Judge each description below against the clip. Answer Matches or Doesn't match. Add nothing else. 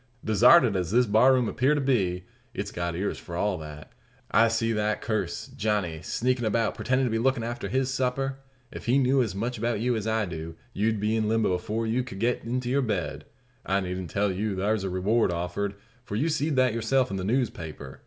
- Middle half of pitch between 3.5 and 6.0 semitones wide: Matches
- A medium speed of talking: Doesn't match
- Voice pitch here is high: Doesn't match